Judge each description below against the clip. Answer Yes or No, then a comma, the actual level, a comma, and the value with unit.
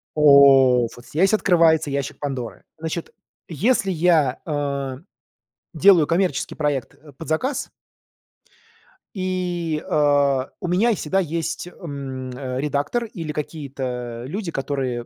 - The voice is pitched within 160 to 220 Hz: No, medium, 150 Hz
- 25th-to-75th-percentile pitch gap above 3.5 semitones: Yes, average, 4.2 semitones